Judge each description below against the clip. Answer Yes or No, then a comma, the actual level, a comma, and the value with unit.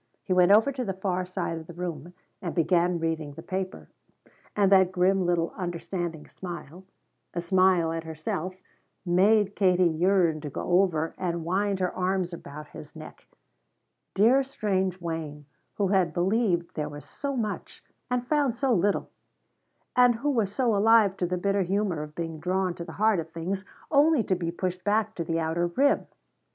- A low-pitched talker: No, medium, 185 Hz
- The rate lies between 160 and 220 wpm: Yes, average, 175 wpm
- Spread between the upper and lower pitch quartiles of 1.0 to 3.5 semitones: Yes, average, 3.1 semitones